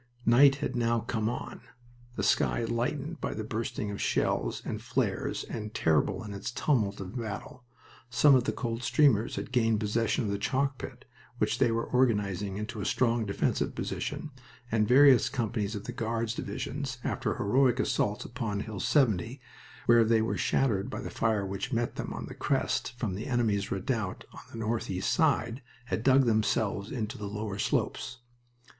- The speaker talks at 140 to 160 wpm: No, average, 175 wpm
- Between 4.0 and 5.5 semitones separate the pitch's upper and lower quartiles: No, average, 3.2 semitones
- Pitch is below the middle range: Yes, low, 115 Hz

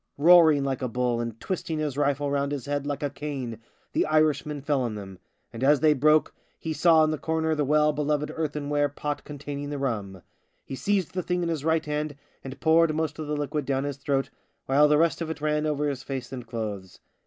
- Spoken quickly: Yes, fast, 230 wpm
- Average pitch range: No, narrow, 2.2 semitones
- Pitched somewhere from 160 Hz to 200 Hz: No, medium, 145 Hz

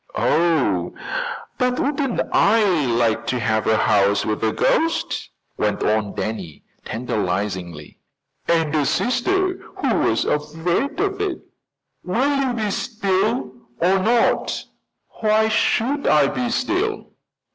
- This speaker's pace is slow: Yes, slow, 120 wpm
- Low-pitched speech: No, medium, 175 Hz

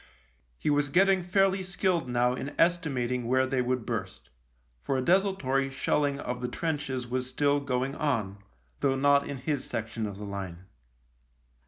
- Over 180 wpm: No, average, 165 wpm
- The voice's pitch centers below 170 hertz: Yes, low, 135 Hz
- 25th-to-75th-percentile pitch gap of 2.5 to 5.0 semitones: Yes, average, 3.3 semitones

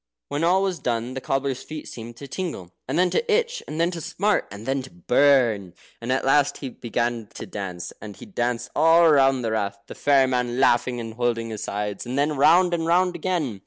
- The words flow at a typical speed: No, fast, 220 wpm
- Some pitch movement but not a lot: No, wide, 5.9 semitones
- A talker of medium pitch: No, low, 130 Hz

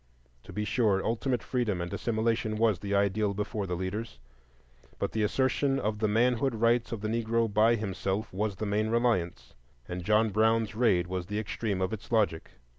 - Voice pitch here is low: Yes, low, 110 Hz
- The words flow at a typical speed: Yes, average, 185 wpm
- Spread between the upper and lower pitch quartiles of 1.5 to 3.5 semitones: Yes, narrow, 2.4 semitones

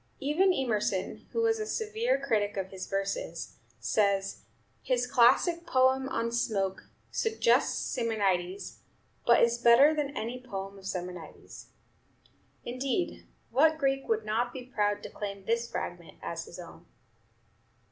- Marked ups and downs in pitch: Yes, wide, 6.0 semitones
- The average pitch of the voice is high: Yes, high, 240 Hz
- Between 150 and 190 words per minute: No, slow, 135 wpm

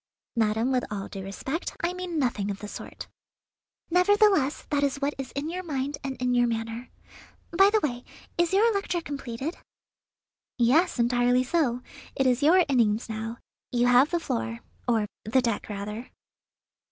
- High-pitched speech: Yes, very high, 255 Hz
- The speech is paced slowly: No, average, 165 wpm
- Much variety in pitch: Yes, wide, 5.8 semitones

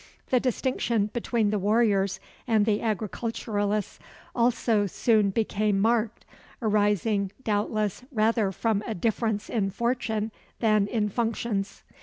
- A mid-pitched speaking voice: No, high, 215 Hz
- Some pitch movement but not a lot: No, narrow, 2.0 semitones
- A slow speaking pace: Yes, slow, 115 wpm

